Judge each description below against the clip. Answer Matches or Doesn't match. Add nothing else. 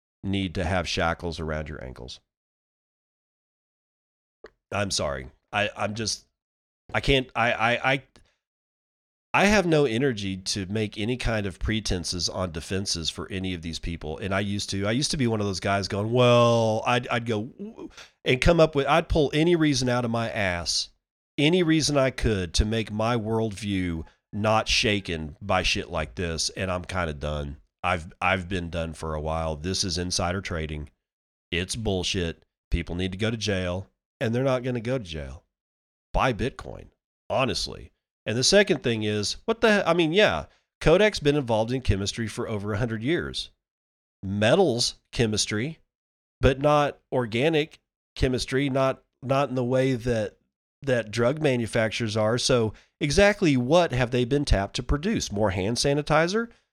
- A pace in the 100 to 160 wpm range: Doesn't match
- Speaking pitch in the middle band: Doesn't match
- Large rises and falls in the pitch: Matches